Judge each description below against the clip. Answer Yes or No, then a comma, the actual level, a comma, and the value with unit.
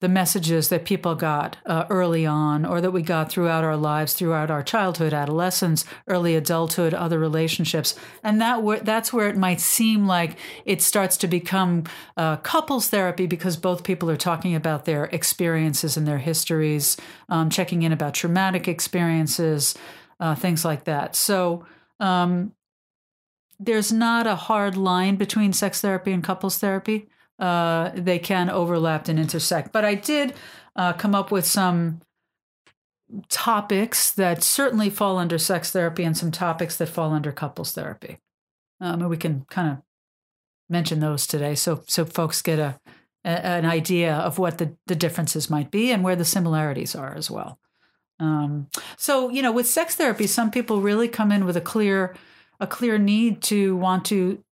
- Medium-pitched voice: Yes, medium, 175 Hz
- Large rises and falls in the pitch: No, average, 3.5 semitones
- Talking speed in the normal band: Yes, average, 170 wpm